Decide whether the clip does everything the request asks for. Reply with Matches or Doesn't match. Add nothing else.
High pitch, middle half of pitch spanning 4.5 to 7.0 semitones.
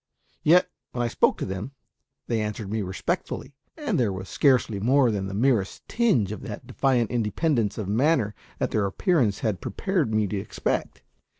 Doesn't match